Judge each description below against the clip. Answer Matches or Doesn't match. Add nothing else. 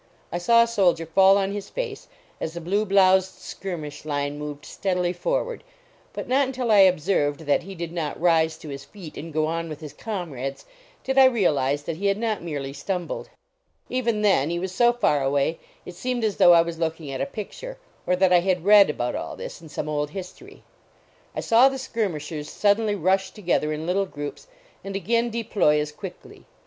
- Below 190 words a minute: Doesn't match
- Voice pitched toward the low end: Doesn't match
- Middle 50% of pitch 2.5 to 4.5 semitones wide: Doesn't match